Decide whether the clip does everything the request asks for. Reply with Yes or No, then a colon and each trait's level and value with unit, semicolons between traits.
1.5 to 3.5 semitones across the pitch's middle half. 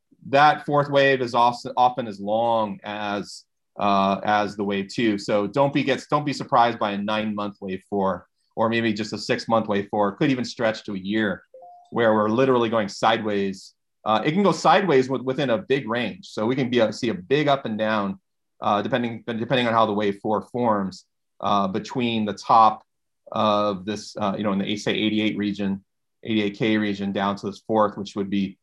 Yes: average, 3.2 semitones